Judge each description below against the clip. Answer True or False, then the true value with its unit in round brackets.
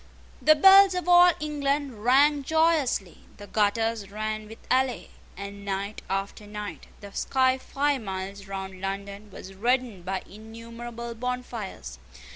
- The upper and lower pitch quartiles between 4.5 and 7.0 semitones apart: True (4.9 semitones)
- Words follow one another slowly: True (130 wpm)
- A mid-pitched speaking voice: False (225 Hz)